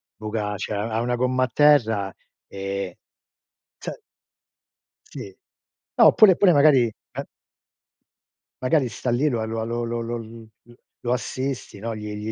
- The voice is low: Yes, low, 115 Hz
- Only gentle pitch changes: No, average, 3.0 semitones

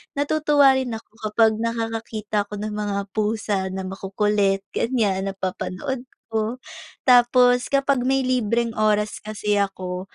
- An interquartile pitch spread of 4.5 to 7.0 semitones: No, average, 3.4 semitones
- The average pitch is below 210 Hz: No, high, 215 Hz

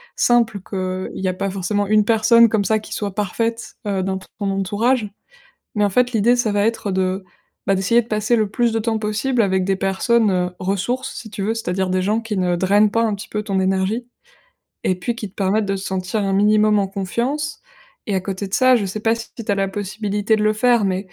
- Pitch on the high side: Yes, high, 205 Hz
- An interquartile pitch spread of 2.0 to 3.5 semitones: Yes, average, 2.8 semitones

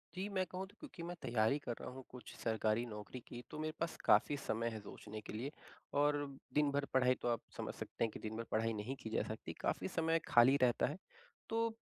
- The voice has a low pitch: Yes, low, 125 Hz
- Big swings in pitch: Yes, wide, 5.7 semitones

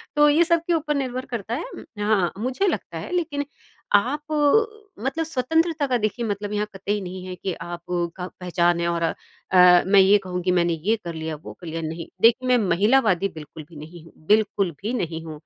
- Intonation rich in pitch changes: Yes, wide, 6.8 semitones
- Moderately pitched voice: No, high, 205 Hz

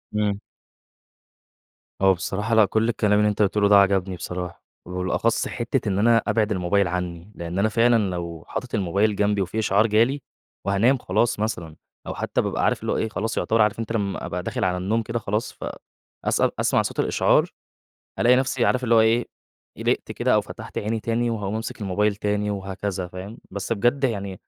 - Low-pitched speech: Yes, low, 105 Hz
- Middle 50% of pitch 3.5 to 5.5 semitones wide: No, average, 2.9 semitones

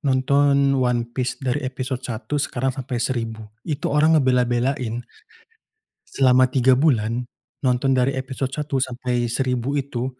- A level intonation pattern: Yes, narrow, 1.9 semitones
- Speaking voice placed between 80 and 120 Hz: No, low, 130 Hz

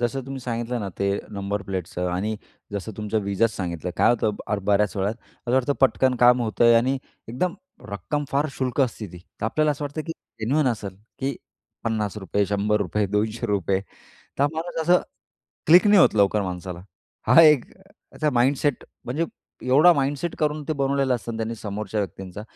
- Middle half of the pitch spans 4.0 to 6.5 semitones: Yes, wide, 5.4 semitones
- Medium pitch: No, low, 115 Hz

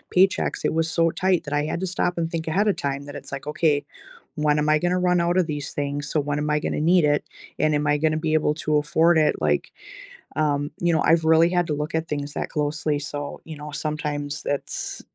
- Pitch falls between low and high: Yes, medium, 155 Hz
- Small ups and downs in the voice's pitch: Yes, narrow, 2.1 semitones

